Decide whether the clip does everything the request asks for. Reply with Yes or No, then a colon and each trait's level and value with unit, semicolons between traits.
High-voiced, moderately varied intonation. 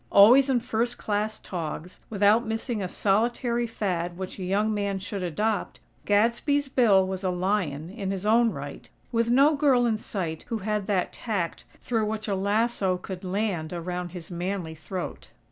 Yes: high, 205 Hz; average, 3.8 semitones